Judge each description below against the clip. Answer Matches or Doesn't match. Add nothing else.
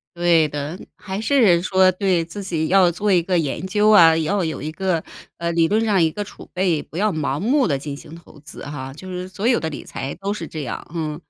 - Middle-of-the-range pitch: Matches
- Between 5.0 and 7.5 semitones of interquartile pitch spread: Doesn't match